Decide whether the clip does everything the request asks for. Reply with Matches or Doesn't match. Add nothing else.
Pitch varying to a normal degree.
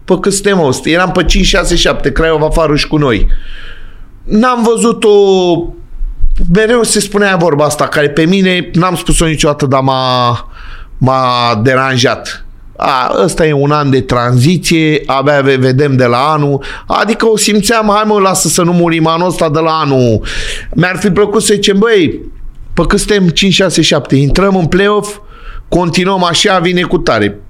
Doesn't match